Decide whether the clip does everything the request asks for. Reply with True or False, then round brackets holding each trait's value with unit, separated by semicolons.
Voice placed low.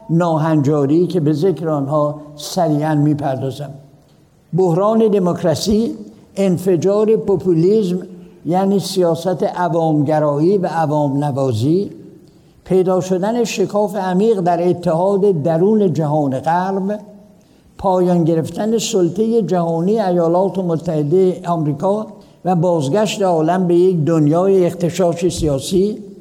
False (180 Hz)